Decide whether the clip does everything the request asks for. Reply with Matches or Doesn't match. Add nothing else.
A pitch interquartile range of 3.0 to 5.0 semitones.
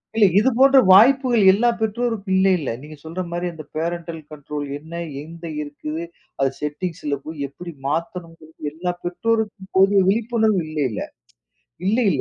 Doesn't match